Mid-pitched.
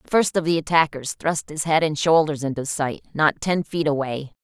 Yes: medium, 155 Hz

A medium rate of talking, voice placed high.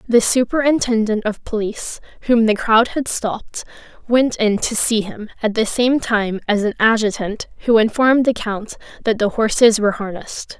Yes: average, 170 wpm; high, 225 Hz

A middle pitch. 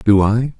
No: low, 110 Hz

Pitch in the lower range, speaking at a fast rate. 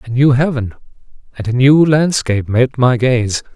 No: low, 130 Hz; average, 170 wpm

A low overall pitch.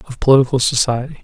Yes: low, 130 Hz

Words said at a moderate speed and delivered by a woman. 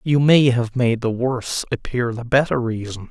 No: average, 195 wpm; male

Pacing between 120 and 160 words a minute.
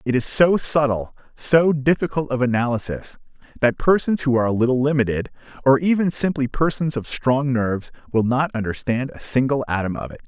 No: average, 175 wpm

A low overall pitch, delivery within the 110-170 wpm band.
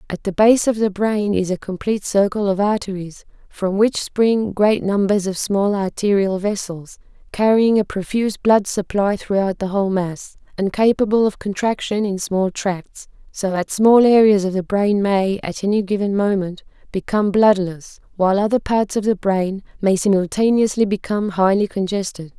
No: high, 200 Hz; average, 165 wpm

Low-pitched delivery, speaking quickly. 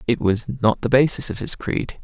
Yes: low, 120 Hz; fast, 235 wpm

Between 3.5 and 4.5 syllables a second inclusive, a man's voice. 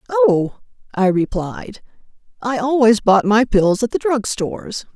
No: 4.0 syllables/s; female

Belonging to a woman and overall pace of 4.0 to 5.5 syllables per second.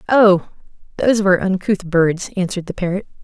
No: female; 5.9 syllables/s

